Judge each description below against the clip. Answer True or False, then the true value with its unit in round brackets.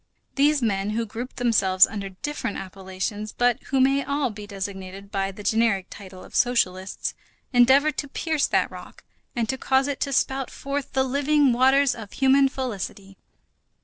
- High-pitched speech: True (240 Hz)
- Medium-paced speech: True (165 wpm)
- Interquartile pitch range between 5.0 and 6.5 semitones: True (5.5 semitones)